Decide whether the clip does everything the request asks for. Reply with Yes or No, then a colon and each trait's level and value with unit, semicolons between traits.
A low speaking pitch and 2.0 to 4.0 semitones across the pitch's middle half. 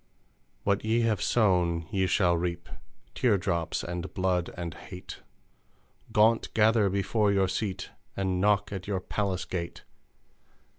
Yes: very low, 95 Hz; average, 2.8 semitones